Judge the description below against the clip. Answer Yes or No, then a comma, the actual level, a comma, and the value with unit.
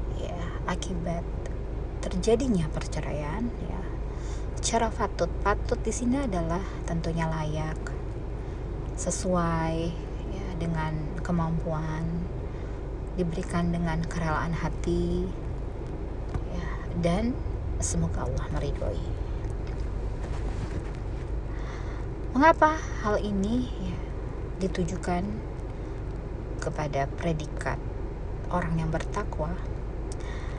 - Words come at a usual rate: No, slow, 70 wpm